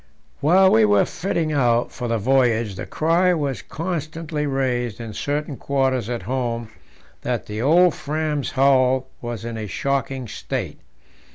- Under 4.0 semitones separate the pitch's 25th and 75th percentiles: No, average, 4.4 semitones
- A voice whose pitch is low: Yes, low, 130 Hz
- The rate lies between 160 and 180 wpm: No, average, 150 wpm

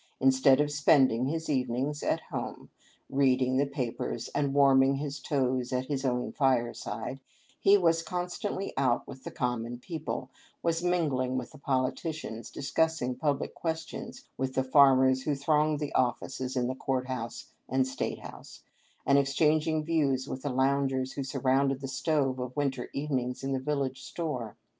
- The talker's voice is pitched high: No, low, 135 Hz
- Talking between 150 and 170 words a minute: Yes, average, 160 wpm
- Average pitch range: No, narrow, 2.3 semitones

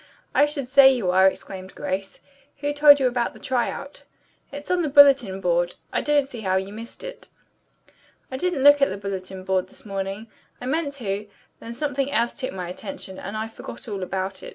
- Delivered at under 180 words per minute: No, fast, 205 wpm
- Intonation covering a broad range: Yes, wide, 6.5 semitones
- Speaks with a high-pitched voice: Yes, high, 230 Hz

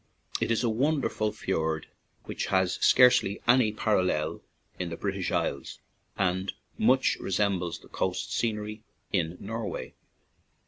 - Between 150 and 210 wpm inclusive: No, slow, 135 wpm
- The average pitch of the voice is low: Yes, low, 100 Hz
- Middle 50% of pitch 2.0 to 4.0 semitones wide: Yes, average, 3.6 semitones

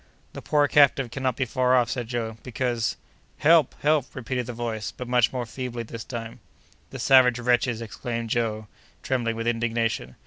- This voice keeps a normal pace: Yes, average, 170 wpm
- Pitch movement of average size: No, narrow, 2.0 semitones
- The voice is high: No, low, 120 Hz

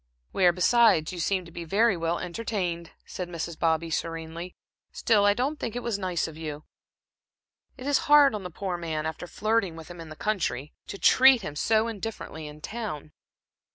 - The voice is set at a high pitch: No, medium, 180 Hz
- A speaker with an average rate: Yes, average, 190 wpm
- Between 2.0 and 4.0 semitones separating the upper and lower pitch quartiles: No, average, 5.1 semitones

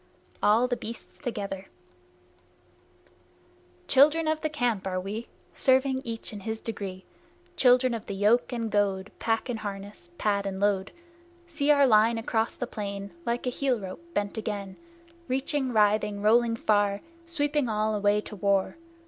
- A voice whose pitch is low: No, high, 220 Hz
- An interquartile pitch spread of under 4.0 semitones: Yes, average, 3.6 semitones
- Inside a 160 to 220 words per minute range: No, average, 150 wpm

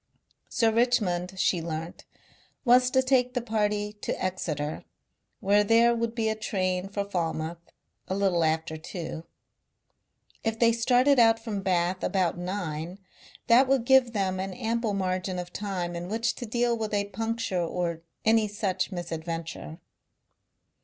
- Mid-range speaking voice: No, high, 200 Hz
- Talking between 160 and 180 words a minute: No, average, 145 wpm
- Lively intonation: No, average, 4.5 semitones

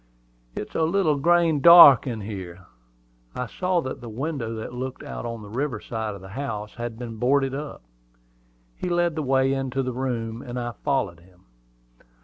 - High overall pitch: No, low, 125 Hz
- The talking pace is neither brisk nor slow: Yes, average, 180 wpm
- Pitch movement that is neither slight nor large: Yes, average, 4.2 semitones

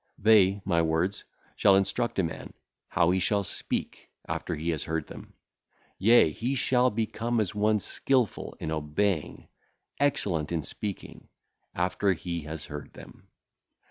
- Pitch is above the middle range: No, very low, 95 Hz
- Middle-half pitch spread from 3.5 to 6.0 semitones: Yes, average, 4.9 semitones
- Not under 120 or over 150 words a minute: Yes, average, 140 wpm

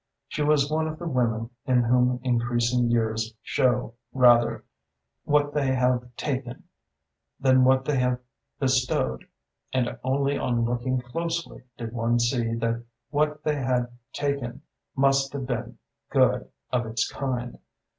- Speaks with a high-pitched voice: No, low, 125 Hz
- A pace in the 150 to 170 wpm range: No, slow, 135 wpm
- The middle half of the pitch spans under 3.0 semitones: Yes, narrow, 2.4 semitones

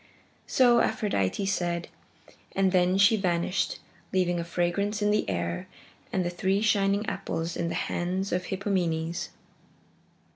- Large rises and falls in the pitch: No, narrow, 2.6 semitones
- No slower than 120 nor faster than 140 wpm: Yes, slow, 135 wpm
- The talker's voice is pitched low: No, medium, 185 Hz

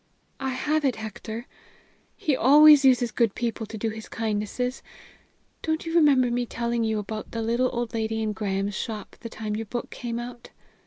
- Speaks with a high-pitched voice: Yes, high, 235 Hz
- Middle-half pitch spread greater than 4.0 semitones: No, narrow, 2.6 semitones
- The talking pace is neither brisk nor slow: Yes, average, 180 wpm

